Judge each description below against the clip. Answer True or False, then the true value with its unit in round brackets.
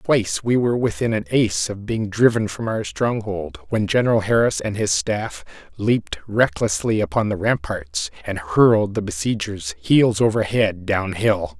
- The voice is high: False (110 Hz)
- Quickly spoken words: False (165 wpm)